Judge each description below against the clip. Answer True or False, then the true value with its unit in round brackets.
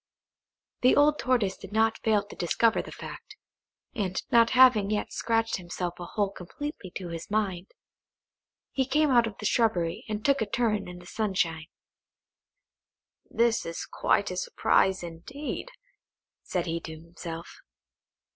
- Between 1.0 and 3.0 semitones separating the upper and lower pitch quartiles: False (4.8 semitones)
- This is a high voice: True (205 Hz)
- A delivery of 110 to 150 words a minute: True (145 wpm)